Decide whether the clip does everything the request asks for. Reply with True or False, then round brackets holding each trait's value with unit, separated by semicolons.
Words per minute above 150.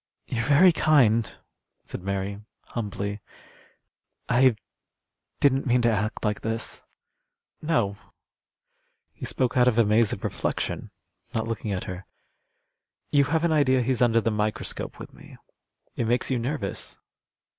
False (135 wpm)